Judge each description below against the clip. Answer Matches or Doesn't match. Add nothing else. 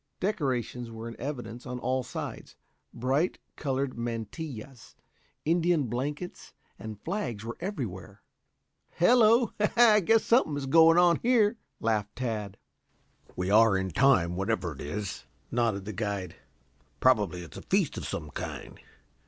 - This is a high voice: Doesn't match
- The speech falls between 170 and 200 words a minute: Doesn't match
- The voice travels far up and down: Matches